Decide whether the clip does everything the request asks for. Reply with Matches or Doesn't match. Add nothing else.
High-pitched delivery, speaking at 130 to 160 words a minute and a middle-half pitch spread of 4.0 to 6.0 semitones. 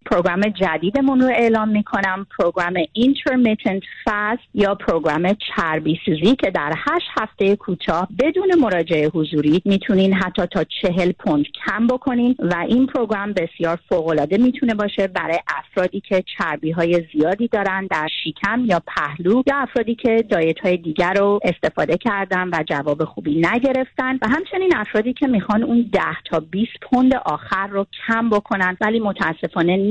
Matches